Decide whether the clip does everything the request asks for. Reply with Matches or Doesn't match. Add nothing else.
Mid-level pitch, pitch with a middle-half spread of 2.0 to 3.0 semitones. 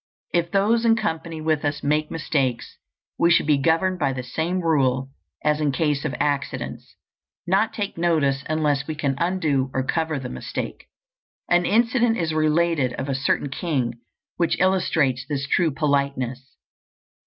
Doesn't match